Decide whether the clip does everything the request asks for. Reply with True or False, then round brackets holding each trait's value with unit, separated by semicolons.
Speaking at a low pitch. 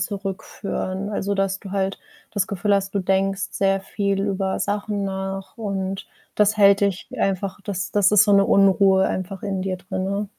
False (195 Hz)